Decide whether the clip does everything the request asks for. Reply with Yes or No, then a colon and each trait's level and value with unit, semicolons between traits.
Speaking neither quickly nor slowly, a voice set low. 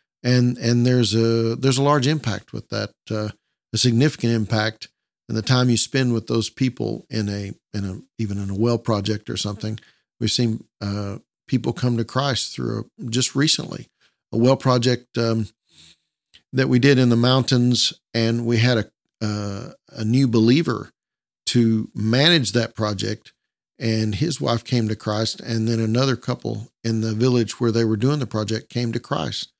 Yes: average, 180 wpm; low, 115 Hz